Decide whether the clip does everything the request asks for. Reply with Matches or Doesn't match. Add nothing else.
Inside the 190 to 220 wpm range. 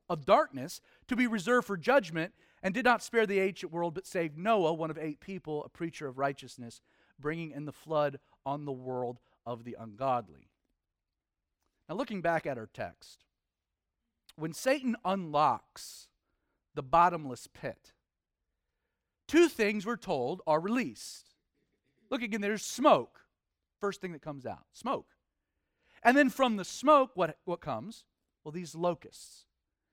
Doesn't match